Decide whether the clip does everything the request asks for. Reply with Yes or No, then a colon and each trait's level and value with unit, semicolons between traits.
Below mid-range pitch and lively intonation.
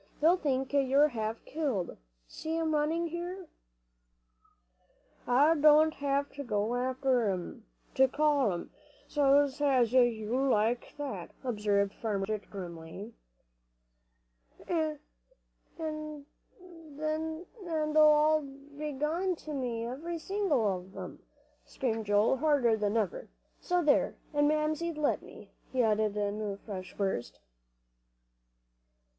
No: very high, 275 Hz; wide, 5.9 semitones